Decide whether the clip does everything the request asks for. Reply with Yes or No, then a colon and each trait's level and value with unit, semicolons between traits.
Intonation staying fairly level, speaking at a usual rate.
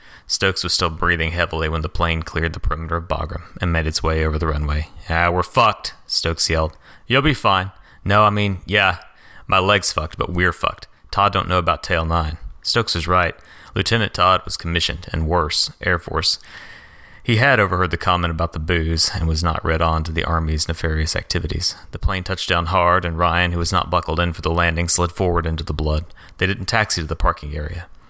No: narrow, 2.1 semitones; fast, 215 wpm